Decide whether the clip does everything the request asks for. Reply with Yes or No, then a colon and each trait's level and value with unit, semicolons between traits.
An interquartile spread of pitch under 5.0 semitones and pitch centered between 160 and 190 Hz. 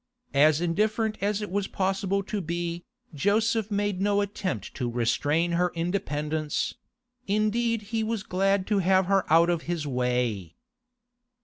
Yes: average, 4.5 semitones; medium, 185 Hz